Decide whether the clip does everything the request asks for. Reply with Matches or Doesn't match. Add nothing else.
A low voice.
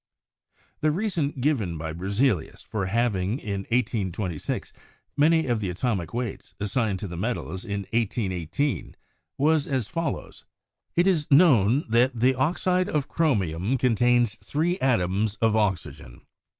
Matches